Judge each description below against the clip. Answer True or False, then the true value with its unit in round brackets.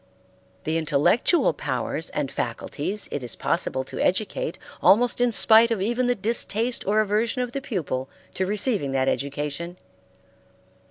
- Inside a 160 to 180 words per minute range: False (145 wpm)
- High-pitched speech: True (210 Hz)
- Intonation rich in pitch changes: True (7.8 semitones)